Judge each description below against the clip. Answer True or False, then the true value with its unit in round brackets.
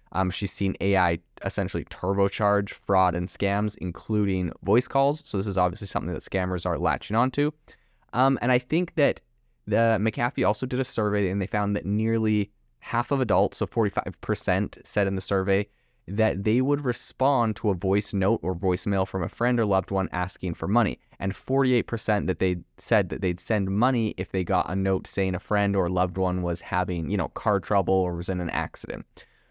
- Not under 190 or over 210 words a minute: True (200 wpm)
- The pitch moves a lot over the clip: False (3.3 semitones)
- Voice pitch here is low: True (100 Hz)